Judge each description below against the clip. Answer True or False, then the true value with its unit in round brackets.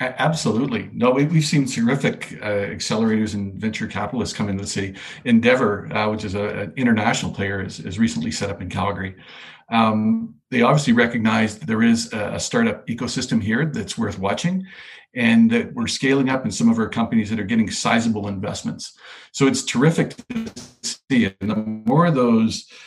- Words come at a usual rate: True (180 wpm)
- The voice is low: True (115 Hz)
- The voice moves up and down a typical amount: False (8.9 semitones)